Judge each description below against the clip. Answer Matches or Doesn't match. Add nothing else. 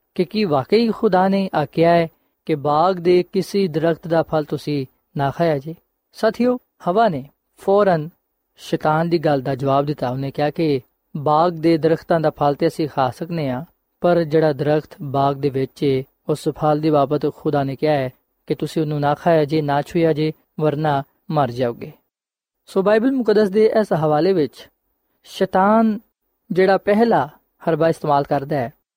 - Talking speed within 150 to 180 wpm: Matches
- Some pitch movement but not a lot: Matches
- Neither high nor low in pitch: Matches